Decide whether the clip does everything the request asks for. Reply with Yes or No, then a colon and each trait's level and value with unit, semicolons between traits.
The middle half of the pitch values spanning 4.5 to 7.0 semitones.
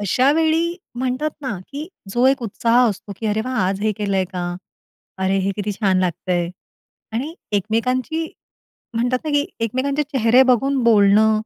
Yes: average, 4.8 semitones